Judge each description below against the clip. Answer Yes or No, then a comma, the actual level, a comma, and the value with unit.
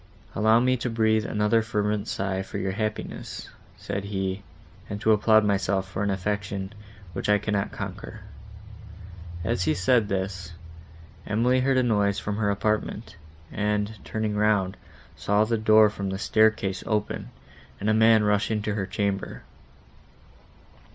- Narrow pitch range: Yes, narrow, 1.8 semitones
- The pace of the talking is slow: No, average, 145 wpm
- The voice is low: Yes, low, 105 Hz